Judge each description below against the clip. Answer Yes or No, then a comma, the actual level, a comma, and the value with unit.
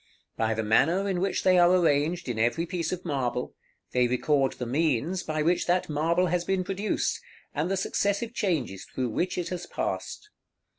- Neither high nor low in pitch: Yes, medium, 170 Hz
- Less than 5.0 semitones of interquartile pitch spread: No, wide, 5.6 semitones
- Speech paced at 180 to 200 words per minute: Yes, average, 185 wpm